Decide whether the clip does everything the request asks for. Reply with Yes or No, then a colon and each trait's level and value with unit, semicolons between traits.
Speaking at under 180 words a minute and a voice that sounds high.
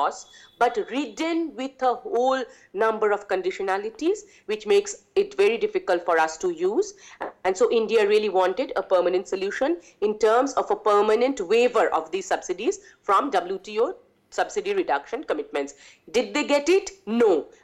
Yes: average, 155 wpm; very high, 315 Hz